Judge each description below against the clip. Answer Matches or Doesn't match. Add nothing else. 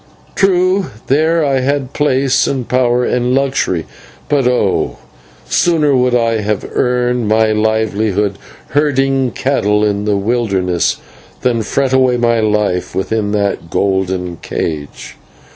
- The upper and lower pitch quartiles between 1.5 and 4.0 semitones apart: Doesn't match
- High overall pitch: Doesn't match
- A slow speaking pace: Matches